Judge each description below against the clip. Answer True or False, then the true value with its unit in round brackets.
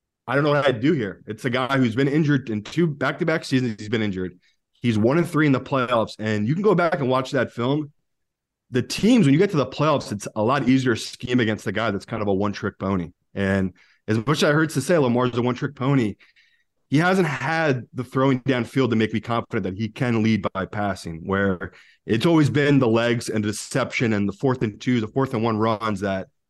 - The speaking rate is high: True (240 wpm)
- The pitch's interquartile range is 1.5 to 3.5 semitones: False (4.5 semitones)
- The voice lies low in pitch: True (125 Hz)